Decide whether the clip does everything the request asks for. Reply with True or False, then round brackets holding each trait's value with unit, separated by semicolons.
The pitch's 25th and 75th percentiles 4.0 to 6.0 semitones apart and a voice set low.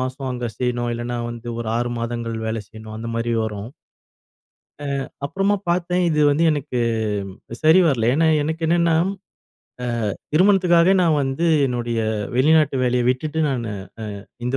True (5.2 semitones; 130 Hz)